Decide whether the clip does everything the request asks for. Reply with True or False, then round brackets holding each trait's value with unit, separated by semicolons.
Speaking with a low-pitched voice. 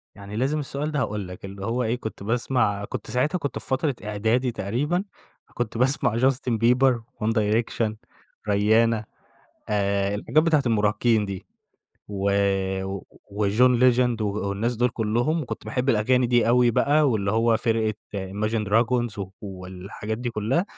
True (115 Hz)